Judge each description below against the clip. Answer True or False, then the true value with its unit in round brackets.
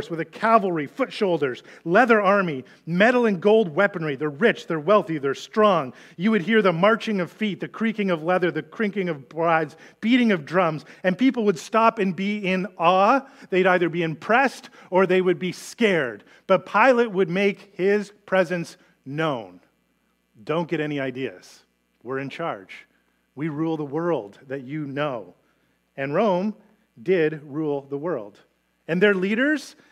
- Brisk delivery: False (165 wpm)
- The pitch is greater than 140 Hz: True (185 Hz)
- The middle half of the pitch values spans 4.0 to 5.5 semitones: True (5.1 semitones)